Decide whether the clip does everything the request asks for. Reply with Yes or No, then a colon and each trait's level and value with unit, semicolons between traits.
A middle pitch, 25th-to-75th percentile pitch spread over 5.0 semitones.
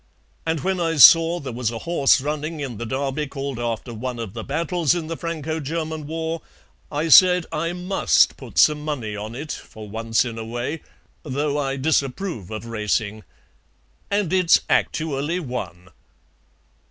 Yes: medium, 145 Hz; wide, 5.5 semitones